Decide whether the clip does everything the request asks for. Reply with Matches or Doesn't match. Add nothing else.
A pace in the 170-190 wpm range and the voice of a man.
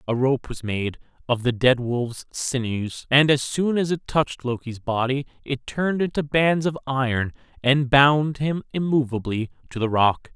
Matches